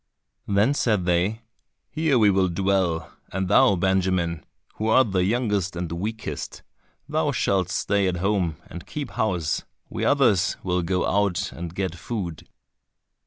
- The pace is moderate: Yes, average, 145 wpm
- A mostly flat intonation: No, average, 3.3 semitones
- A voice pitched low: Yes, very low, 95 Hz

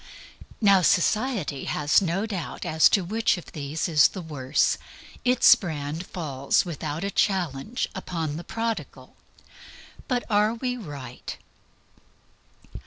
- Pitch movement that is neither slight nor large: No, wide, 6.1 semitones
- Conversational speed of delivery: No, slow, 125 wpm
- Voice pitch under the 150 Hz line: No, medium, 175 Hz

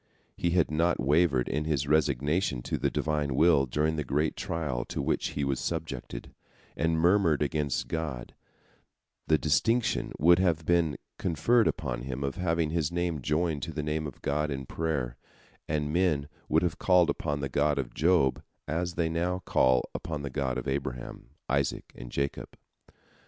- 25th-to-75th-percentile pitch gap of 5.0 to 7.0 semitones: No, average, 3.2 semitones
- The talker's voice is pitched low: Yes, very low, 75 Hz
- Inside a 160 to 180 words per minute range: Yes, average, 170 wpm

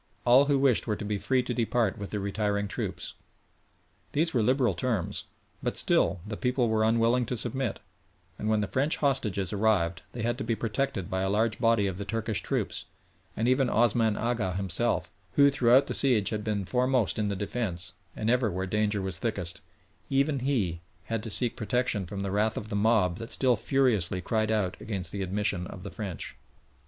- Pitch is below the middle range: Yes, low, 110 Hz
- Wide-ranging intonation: No, average, 3.6 semitones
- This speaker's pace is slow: No, average, 195 wpm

